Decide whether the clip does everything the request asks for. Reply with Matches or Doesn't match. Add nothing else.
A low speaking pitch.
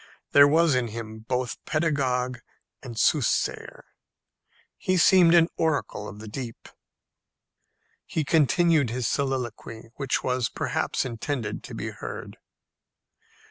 Matches